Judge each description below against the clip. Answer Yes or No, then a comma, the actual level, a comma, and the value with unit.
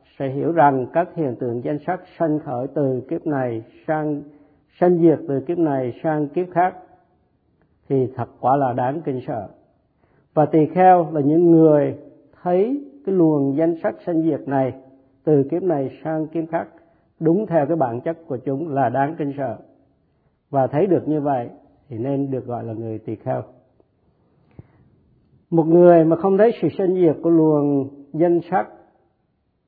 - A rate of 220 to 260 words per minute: No, average, 170 wpm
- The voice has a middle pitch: Yes, medium, 150 Hz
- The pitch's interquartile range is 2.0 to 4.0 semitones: Yes, average, 3.6 semitones